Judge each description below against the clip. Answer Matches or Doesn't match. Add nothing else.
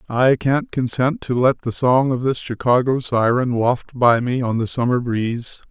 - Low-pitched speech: Matches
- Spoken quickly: Doesn't match